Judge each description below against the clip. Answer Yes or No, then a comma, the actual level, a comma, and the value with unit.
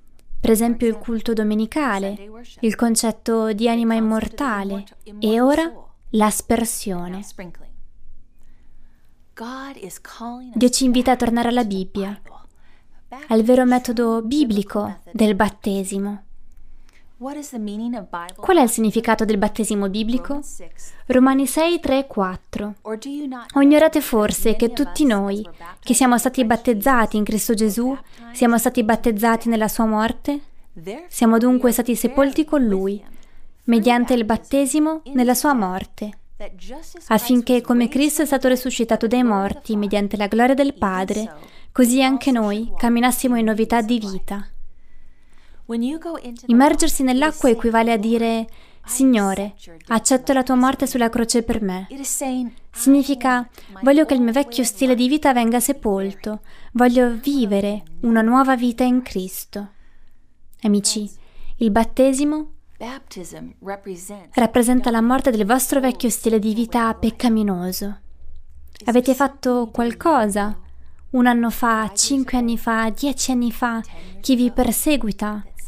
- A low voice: No, high, 235 Hz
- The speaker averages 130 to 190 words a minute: No, average, 120 wpm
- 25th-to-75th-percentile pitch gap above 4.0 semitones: No, average, 3.2 semitones